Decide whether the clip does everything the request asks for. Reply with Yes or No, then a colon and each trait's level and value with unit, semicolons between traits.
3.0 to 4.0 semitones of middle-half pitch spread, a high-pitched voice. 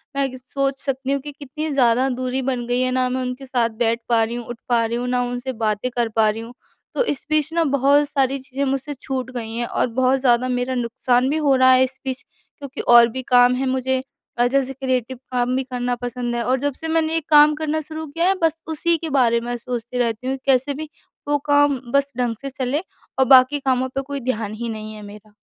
No: narrow, 2.4 semitones; very high, 260 Hz